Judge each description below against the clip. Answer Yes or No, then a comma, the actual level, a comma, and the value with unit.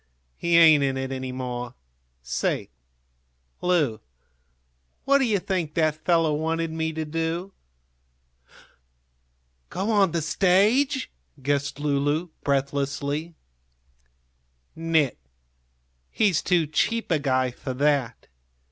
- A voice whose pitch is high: No, medium, 155 Hz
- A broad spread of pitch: No, average, 3.7 semitones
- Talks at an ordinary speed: No, slow, 105 wpm